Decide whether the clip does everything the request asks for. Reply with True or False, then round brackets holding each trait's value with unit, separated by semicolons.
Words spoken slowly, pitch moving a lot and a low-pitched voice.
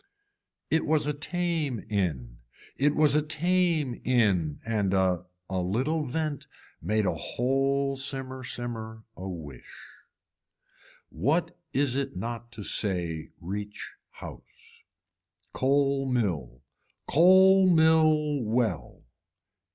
True (105 wpm; 7.0 semitones; 130 Hz)